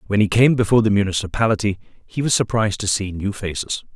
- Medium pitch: No, low, 105 Hz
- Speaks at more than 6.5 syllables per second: Yes, 6.7 syllables/s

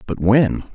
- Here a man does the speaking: Yes, male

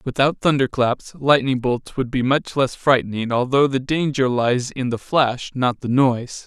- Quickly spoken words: No, average, 175 wpm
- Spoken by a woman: No, male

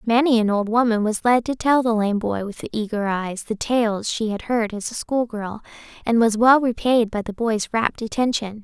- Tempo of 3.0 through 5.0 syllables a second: Yes, 4.8 syllables/s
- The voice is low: No, high, 225 Hz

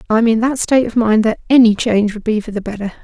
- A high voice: Yes, high, 220 Hz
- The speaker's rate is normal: No, fast, 275 wpm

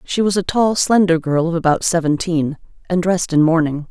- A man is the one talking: No, female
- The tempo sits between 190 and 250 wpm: Yes, average, 200 wpm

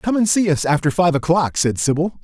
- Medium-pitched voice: Yes, medium, 165 Hz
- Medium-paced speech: No, fast, 240 wpm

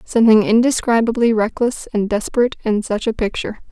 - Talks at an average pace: Yes, average, 145 wpm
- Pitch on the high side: Yes, high, 225 Hz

